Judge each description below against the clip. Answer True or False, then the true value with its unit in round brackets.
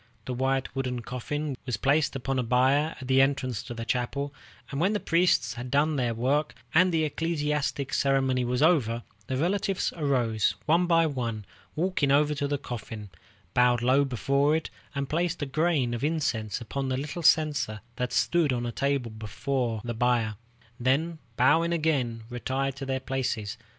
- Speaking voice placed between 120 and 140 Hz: True (135 Hz)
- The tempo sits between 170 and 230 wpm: True (175 wpm)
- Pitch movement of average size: True (3.6 semitones)